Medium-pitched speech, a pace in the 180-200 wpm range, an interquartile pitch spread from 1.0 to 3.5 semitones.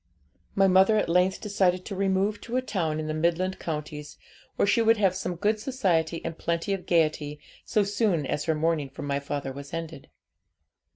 No: medium, 175 Hz; average, 190 wpm; average, 4.3 semitones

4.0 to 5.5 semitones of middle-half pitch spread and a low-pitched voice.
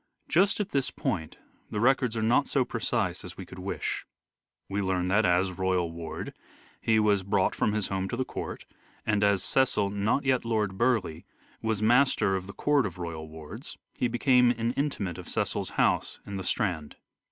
Yes: average, 4.5 semitones; low, 105 Hz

